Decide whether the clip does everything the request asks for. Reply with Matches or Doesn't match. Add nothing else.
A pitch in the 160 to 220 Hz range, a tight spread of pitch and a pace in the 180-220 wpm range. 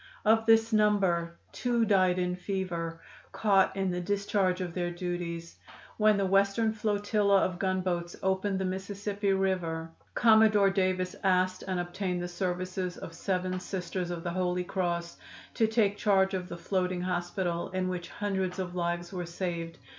Doesn't match